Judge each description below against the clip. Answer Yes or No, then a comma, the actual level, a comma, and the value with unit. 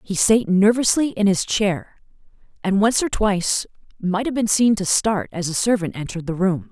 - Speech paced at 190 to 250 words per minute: Yes, average, 195 wpm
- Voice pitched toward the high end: Yes, high, 200 Hz